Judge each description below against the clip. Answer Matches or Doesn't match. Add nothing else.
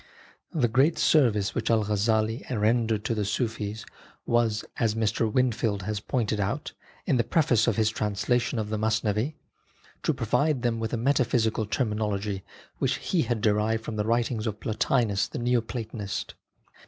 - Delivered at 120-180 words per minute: Matches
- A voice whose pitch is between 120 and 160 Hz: Doesn't match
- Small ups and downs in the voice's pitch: Matches